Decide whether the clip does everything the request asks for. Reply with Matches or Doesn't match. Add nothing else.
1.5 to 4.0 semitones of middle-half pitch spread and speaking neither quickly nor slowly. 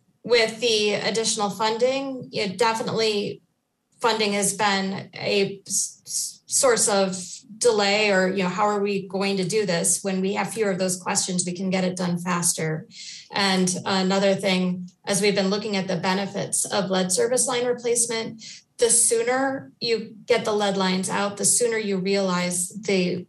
Matches